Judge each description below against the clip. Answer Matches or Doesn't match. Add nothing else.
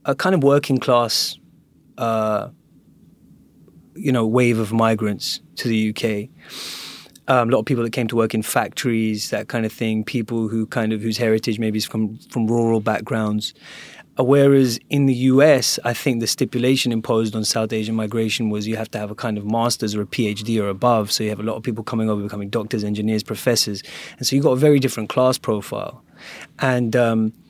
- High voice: Doesn't match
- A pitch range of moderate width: Doesn't match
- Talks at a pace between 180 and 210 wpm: Matches